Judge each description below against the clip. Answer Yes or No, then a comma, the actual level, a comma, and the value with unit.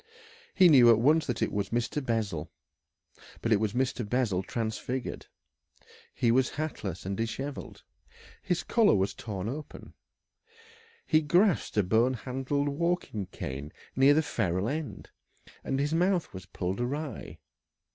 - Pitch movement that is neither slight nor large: No, wide, 5.9 semitones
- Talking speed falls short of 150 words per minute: Yes, average, 140 wpm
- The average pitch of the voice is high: No, low, 125 Hz